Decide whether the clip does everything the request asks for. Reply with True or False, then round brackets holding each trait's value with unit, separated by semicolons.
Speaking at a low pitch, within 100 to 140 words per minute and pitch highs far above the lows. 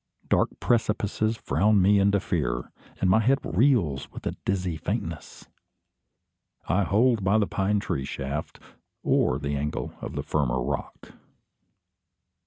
True (95 Hz; 135 wpm; 6.0 semitones)